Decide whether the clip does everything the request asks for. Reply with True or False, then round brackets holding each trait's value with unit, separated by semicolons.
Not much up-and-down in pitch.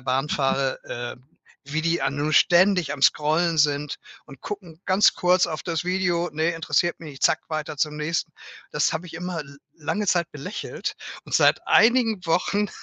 False (3.2 semitones)